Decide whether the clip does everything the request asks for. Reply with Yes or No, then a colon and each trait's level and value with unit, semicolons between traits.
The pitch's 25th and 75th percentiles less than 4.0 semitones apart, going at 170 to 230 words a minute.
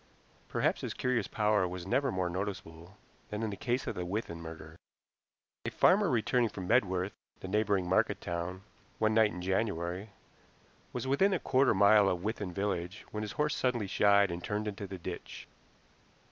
Yes: average, 3.3 semitones; average, 180 wpm